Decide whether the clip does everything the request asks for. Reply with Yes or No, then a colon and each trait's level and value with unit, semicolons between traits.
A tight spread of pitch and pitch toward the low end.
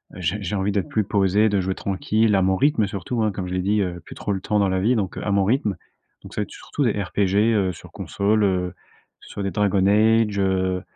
Yes: narrow, 2.1 semitones; low, 100 Hz